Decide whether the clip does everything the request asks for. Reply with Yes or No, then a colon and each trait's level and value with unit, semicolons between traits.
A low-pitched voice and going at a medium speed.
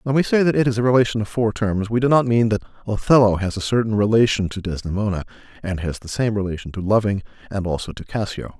No: low, 110 Hz; fast, 235 wpm